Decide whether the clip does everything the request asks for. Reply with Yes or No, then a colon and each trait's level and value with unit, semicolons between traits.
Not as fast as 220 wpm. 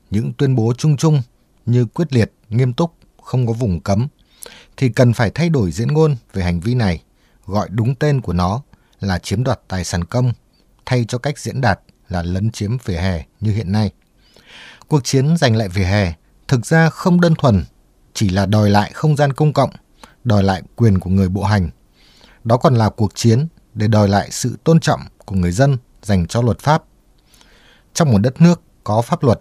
Yes: average, 205 wpm